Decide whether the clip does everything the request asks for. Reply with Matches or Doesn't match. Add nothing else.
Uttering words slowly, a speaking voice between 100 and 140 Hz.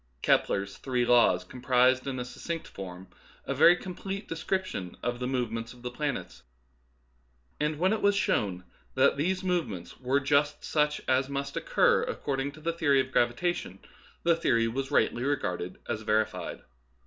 Doesn't match